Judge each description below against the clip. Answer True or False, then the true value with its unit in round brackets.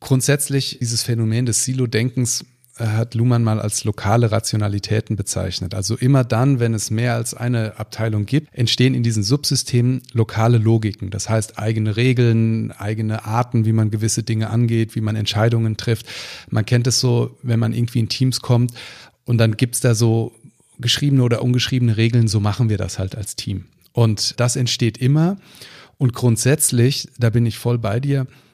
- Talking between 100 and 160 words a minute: False (175 wpm)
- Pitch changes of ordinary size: False (2.1 semitones)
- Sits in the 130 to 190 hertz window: False (115 Hz)